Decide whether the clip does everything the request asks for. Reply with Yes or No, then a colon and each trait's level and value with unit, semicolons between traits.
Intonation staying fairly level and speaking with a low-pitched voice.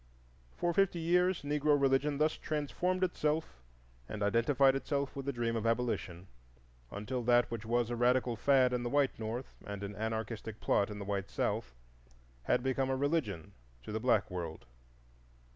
No: average, 4.6 semitones; low, 125 Hz